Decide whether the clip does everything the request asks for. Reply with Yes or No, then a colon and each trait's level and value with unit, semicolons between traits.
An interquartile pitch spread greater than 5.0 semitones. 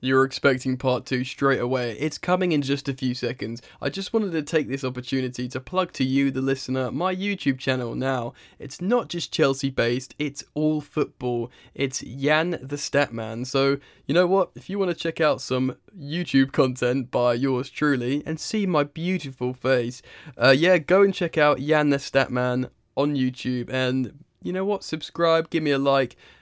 No: average, 3.7 semitones